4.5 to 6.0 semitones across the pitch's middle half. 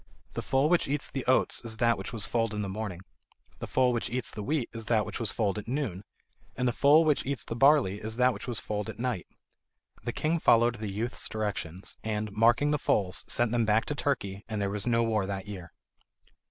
No: average, 3.5 semitones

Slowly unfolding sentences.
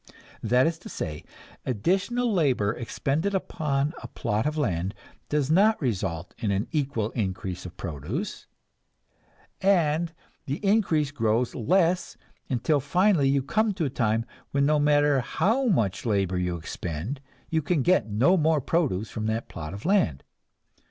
No: average, 150 wpm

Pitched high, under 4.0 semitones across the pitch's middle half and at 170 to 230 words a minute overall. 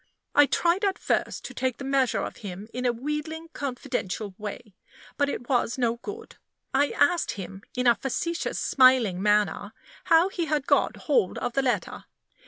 No: very high, 260 Hz; average, 4.9 semitones; average, 175 wpm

